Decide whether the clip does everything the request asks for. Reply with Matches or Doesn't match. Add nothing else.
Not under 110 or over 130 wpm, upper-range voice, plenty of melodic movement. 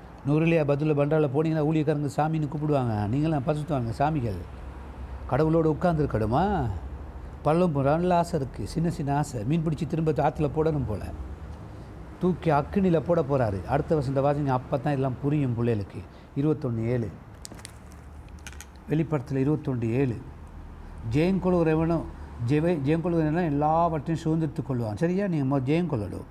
Doesn't match